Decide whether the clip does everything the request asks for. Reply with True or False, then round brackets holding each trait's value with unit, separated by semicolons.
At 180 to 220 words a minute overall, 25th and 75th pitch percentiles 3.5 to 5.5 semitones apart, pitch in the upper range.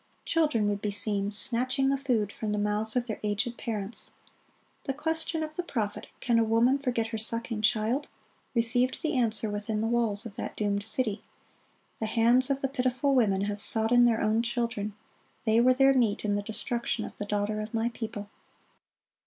False (185 wpm; 3.1 semitones; 230 Hz)